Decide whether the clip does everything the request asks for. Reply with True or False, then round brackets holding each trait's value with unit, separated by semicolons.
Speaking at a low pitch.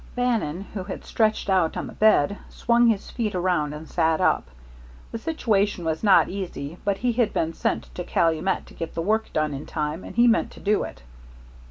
False (190 Hz)